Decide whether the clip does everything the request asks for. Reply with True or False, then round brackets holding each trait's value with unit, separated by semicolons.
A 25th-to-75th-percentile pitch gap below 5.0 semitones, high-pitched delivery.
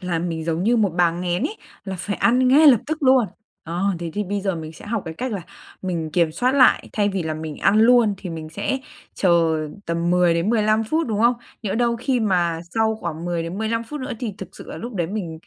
False (5.4 semitones; 195 Hz)